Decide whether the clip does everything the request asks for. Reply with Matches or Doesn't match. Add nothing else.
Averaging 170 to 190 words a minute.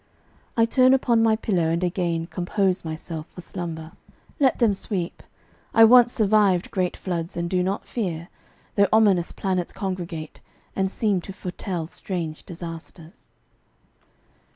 Doesn't match